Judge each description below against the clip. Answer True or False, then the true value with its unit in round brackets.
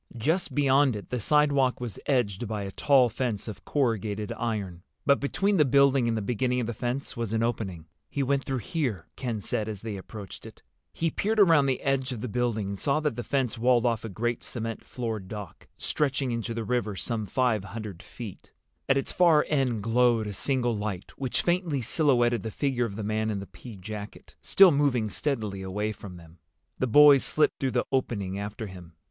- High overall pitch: False (120 Hz)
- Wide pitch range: False (4.4 semitones)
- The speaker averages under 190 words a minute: False (205 wpm)